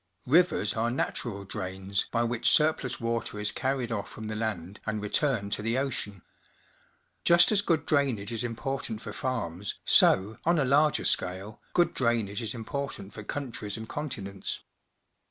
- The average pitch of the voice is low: Yes, low, 115 Hz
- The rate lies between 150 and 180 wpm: Yes, average, 160 wpm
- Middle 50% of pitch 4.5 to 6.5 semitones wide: Yes, average, 4.9 semitones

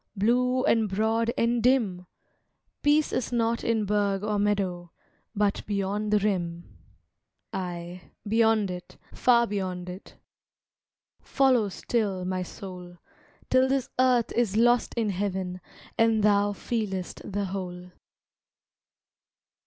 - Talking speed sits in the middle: No, slow, 115 wpm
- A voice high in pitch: Yes, high, 205 Hz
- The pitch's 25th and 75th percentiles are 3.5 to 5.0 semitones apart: Yes, average, 3.8 semitones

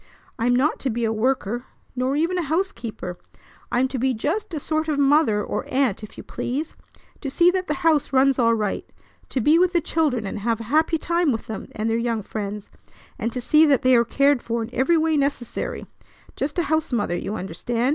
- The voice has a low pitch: No, very high, 260 Hz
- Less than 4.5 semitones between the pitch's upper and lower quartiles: No, average, 5.2 semitones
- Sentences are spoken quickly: Yes, fast, 215 wpm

